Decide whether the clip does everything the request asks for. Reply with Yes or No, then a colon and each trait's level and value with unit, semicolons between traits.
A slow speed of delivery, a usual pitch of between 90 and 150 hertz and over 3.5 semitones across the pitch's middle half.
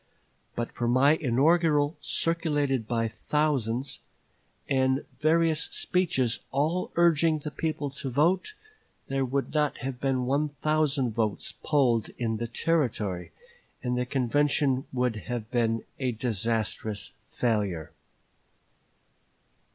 Yes: slow, 110 wpm; low, 135 Hz; average, 4.3 semitones